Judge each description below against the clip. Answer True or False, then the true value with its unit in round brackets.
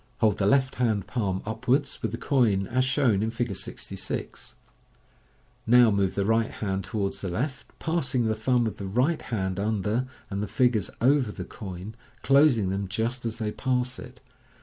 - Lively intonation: False (4.2 semitones)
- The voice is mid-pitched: False (110 Hz)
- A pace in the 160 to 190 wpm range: True (185 wpm)